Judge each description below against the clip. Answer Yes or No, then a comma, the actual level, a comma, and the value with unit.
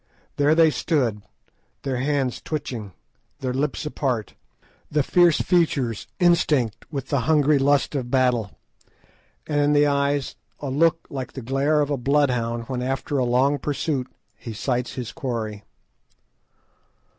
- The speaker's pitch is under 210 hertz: Yes, low, 135 Hz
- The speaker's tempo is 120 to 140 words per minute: Yes, slow, 135 wpm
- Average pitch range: Yes, average, 3.0 semitones